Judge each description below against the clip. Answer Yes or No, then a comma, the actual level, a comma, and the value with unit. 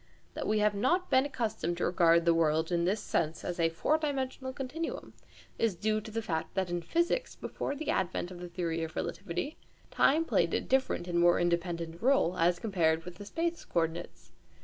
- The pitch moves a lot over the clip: Yes, wide, 7.5 semitones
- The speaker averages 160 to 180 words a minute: No, average, 195 wpm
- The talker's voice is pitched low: No, medium, 180 Hz